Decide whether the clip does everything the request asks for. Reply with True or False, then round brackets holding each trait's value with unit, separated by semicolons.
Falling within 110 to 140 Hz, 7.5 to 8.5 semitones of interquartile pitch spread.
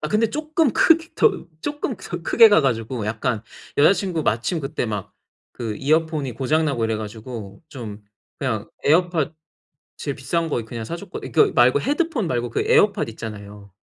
True (135 Hz; 7.9 semitones)